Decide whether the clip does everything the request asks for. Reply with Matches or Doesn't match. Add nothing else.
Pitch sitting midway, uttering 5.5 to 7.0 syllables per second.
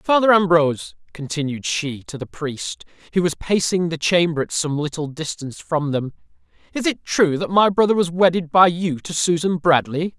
Doesn't match